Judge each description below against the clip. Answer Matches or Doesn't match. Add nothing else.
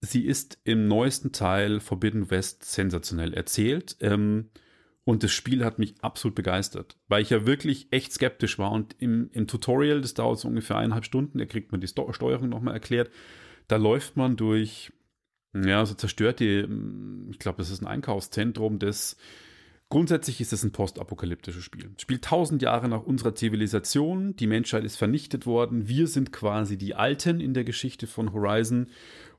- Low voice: Matches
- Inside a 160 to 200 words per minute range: Matches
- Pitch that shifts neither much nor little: Matches